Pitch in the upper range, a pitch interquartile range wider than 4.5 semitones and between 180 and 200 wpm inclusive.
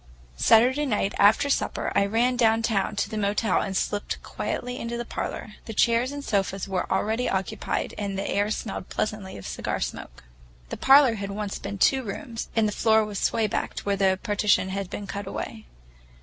No: high, 210 Hz; average, 2.8 semitones; average, 190 wpm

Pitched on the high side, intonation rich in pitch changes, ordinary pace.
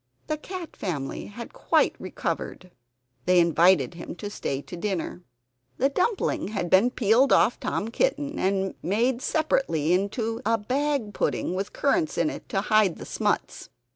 Yes: high, 215 Hz; wide, 6.6 semitones; average, 155 wpm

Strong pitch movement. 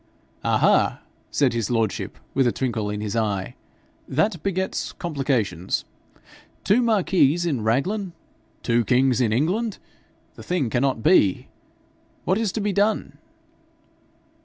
Yes: wide, 8.6 semitones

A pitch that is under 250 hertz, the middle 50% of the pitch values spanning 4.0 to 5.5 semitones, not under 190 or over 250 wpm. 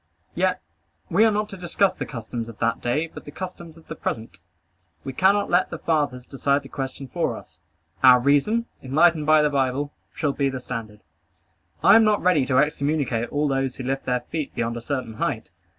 Yes: medium, 140 Hz; average, 4.4 semitones; average, 200 wpm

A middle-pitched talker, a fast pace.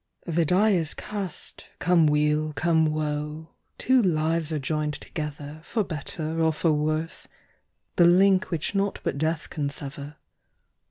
No: medium, 155 Hz; average, 145 wpm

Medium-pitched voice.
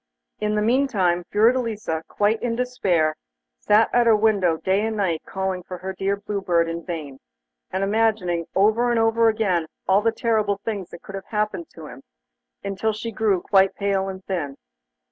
No: high, 200 Hz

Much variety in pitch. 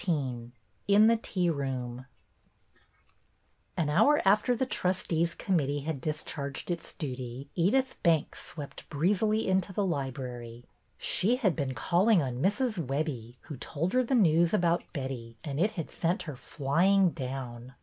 Yes: wide, 6.2 semitones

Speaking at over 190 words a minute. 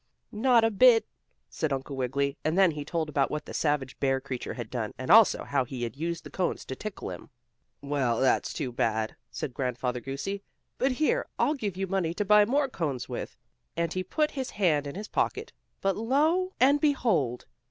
Yes: average, 200 wpm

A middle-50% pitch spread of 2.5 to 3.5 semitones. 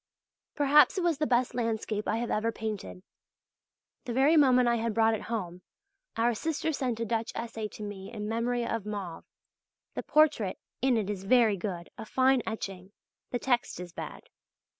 Yes: average, 3.1 semitones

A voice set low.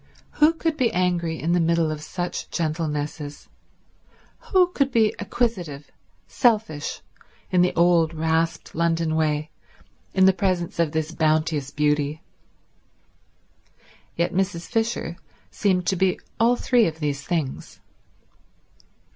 No: medium, 170 Hz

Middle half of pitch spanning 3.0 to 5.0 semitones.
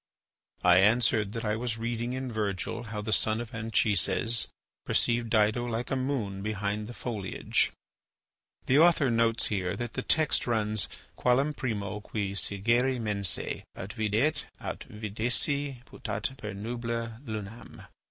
No: narrow, 2.6 semitones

